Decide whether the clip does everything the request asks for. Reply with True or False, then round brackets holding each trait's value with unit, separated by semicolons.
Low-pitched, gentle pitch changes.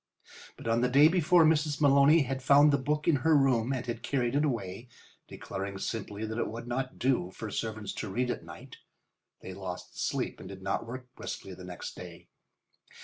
False (125 Hz; 4.5 semitones)